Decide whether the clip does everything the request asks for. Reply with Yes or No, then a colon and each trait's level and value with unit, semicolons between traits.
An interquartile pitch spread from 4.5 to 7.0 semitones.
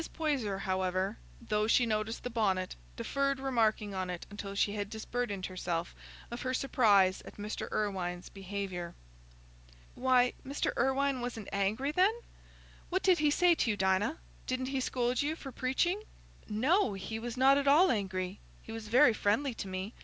Yes: average, 5.2 semitones